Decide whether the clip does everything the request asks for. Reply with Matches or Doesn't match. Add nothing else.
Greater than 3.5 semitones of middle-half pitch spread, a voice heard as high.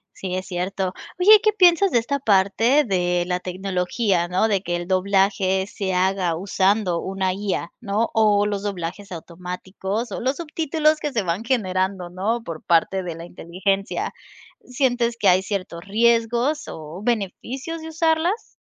Matches